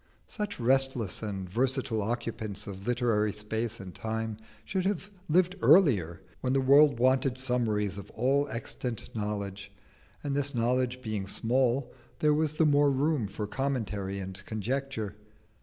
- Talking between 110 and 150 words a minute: Yes, average, 140 wpm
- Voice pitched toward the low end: Yes, low, 120 Hz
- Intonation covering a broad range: No, average, 4.6 semitones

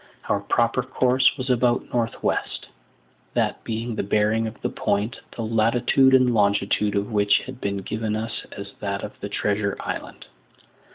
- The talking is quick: No, average, 165 wpm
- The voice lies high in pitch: No, low, 110 Hz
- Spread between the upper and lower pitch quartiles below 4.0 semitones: Yes, average, 2.9 semitones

